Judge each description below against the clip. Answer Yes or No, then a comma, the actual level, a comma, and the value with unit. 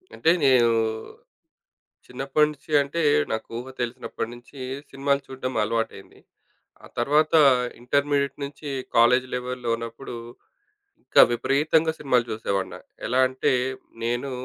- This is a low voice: Yes, low, 130 Hz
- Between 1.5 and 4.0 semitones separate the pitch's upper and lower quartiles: Yes, average, 2.9 semitones